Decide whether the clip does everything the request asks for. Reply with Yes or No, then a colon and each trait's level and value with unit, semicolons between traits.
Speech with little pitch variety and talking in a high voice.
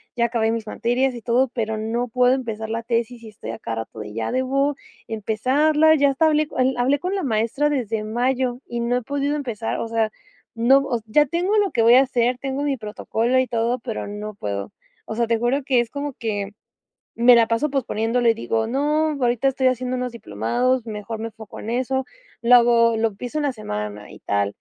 No: average, 3.0 semitones; high, 240 Hz